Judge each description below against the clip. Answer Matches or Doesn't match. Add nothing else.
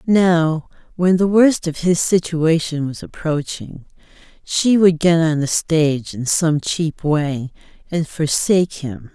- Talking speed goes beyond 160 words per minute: Doesn't match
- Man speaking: Doesn't match